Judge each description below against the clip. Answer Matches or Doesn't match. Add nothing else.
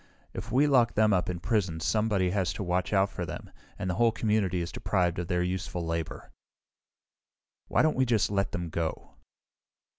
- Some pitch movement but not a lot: Matches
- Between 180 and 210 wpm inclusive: Matches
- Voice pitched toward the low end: Matches